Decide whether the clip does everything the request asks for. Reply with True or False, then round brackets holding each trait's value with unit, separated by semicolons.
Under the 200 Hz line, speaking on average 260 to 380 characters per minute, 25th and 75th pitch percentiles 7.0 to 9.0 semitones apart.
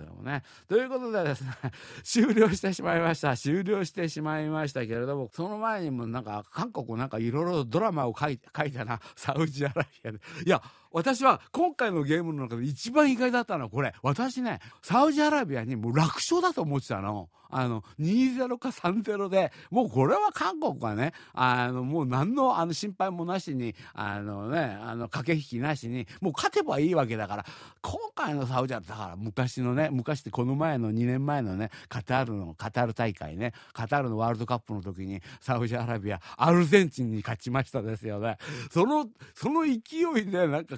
True (140 Hz; 375 characters per minute; 8.0 semitones)